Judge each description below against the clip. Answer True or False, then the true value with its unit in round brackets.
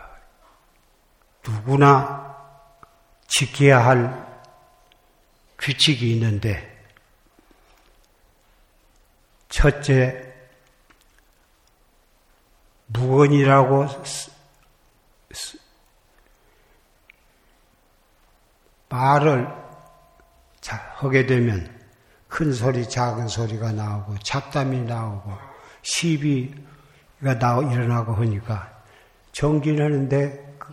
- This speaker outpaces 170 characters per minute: False (115 characters per minute)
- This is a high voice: False (130 Hz)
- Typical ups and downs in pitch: True (3.4 semitones)